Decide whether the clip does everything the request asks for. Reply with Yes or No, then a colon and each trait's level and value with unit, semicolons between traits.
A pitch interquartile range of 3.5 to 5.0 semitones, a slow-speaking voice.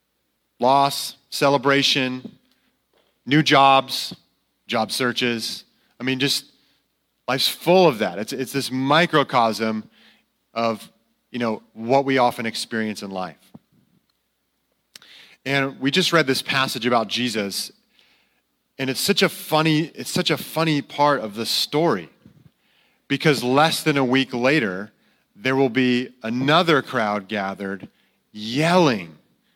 Yes: average, 3.8 semitones; slow, 120 wpm